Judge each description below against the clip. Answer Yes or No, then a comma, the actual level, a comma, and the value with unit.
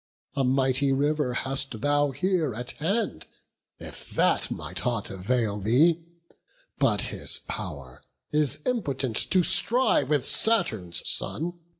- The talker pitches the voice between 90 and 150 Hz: Yes, low, 135 Hz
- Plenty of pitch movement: Yes, wide, 5.7 semitones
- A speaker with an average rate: No, slow, 120 wpm